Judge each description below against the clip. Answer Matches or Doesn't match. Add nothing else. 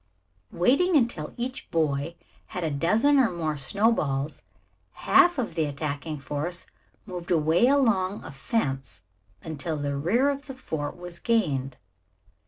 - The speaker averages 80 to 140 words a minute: Matches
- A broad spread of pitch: Matches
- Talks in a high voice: Doesn't match